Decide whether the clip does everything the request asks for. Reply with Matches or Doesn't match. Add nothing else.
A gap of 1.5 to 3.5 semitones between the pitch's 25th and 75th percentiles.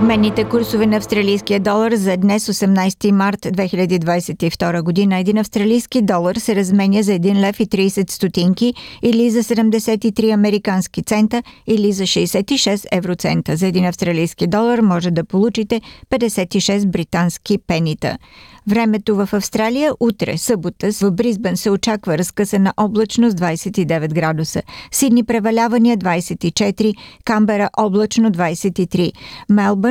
Matches